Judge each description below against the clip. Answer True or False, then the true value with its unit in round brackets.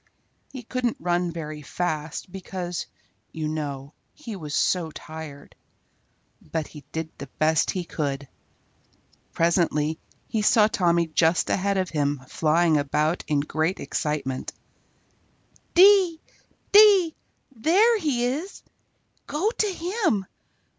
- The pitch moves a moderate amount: False (8.0 semitones)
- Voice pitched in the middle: True (170 Hz)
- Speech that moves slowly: True (120 wpm)